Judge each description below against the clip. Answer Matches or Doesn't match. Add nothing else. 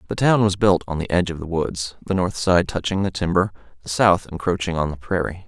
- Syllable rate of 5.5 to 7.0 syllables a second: Matches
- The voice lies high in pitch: Doesn't match